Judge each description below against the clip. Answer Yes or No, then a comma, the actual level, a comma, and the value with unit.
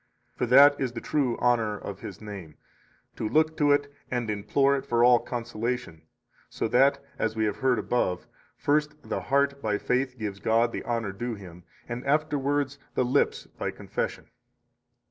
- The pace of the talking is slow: No, average, 170 wpm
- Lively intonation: No, average, 4.3 semitones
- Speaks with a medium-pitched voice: No, low, 120 Hz